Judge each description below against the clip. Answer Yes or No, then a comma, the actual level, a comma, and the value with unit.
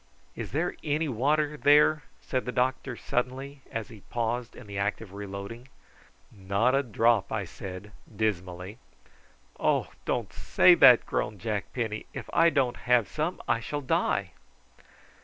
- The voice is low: Yes, low, 120 Hz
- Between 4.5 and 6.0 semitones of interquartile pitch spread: Yes, average, 4.9 semitones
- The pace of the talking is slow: No, average, 150 wpm